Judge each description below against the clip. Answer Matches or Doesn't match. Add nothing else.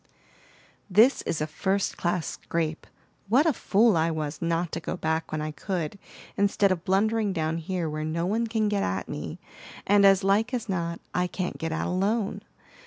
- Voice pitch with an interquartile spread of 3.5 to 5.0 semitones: Matches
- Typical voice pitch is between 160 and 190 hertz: Matches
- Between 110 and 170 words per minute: Doesn't match